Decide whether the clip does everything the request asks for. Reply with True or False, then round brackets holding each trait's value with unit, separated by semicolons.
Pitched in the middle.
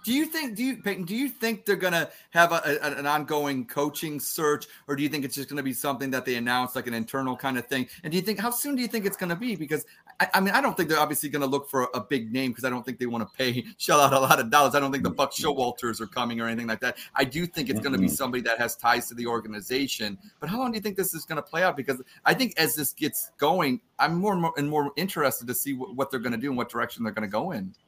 True (145 Hz)